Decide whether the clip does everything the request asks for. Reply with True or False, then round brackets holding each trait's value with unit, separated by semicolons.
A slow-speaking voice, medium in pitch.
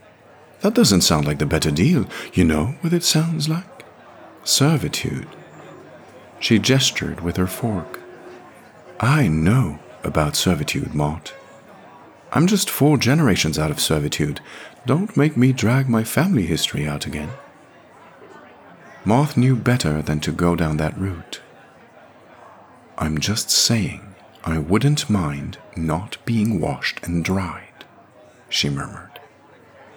False (125 wpm; 95 Hz)